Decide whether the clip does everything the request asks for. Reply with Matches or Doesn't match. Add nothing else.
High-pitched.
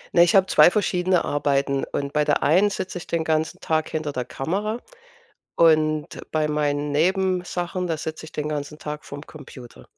Doesn't match